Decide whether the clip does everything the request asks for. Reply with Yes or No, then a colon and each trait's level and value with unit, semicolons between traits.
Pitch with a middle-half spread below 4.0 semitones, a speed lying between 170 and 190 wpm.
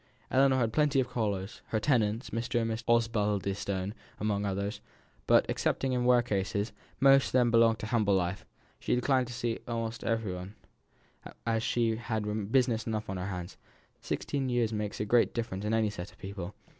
Yes: average, 2.9 semitones; average, 180 wpm